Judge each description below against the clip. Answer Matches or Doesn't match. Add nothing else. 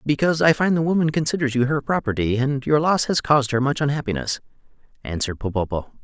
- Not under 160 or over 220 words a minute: Matches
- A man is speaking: Matches